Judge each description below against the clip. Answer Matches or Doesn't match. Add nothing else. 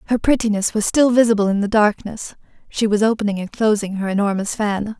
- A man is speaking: Doesn't match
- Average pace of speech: Matches